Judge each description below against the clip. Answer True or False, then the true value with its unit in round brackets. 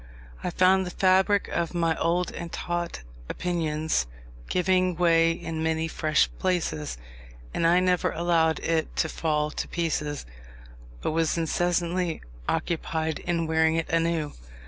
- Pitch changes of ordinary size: False (1.6 semitones)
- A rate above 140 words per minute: False (135 wpm)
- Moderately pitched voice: True (165 Hz)